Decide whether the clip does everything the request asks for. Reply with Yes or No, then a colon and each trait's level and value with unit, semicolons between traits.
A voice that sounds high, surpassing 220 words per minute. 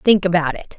No: medium, 180 Hz; fast, 230 wpm